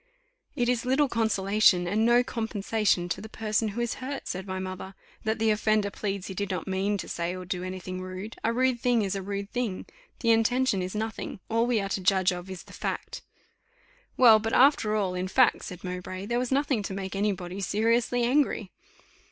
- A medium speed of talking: No, fast, 210 wpm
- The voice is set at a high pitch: Yes, high, 210 Hz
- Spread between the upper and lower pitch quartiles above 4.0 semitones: No, average, 3.6 semitones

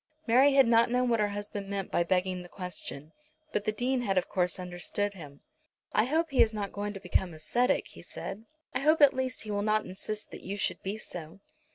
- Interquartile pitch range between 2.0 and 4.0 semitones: No, average, 4.4 semitones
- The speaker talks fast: Yes, fast, 230 wpm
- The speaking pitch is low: No, high, 205 Hz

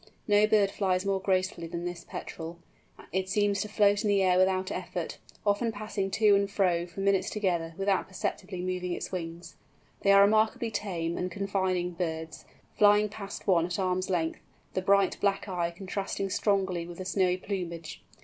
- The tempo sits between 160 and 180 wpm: Yes, average, 175 wpm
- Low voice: No, high, 190 Hz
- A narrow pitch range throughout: Yes, narrow, 2.2 semitones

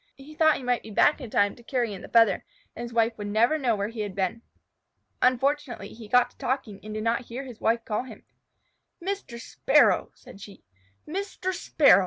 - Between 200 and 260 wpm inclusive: Yes, fast, 205 wpm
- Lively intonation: No, average, 4.0 semitones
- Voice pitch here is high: Yes, high, 235 Hz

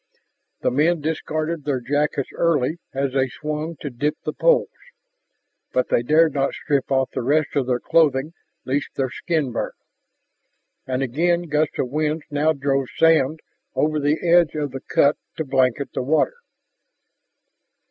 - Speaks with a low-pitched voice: No, medium, 150 Hz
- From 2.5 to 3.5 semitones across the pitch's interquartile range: Yes, average, 2.9 semitones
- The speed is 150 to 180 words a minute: Yes, average, 155 wpm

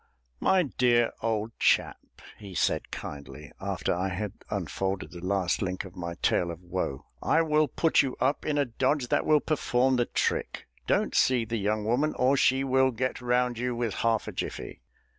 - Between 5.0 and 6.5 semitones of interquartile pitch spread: Yes, average, 5.3 semitones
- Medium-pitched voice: No, low, 120 Hz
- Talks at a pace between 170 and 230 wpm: Yes, average, 185 wpm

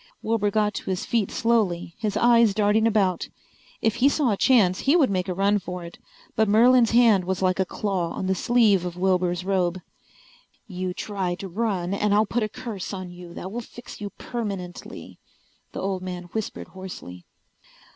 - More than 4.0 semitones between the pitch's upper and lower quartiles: No, average, 3.4 semitones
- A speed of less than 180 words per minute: No, average, 185 wpm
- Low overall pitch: No, high, 195 Hz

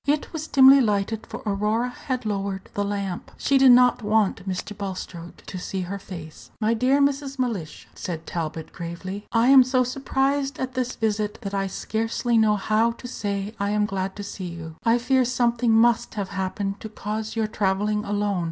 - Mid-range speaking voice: No, high, 210 Hz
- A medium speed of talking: Yes, average, 190 wpm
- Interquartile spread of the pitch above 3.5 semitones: Yes, average, 4.0 semitones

